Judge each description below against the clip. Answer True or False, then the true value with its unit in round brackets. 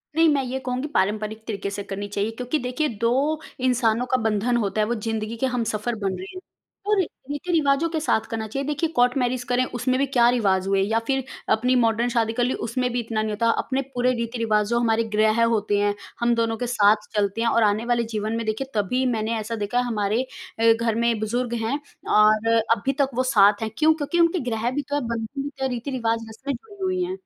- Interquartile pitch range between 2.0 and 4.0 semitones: True (3.0 semitones)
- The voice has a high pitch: True (235 Hz)